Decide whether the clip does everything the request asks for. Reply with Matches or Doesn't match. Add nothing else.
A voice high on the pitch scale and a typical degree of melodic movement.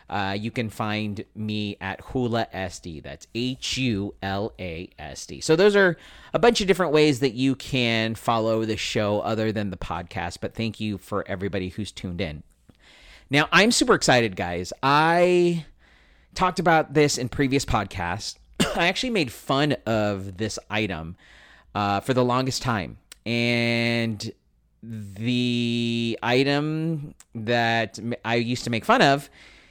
Doesn't match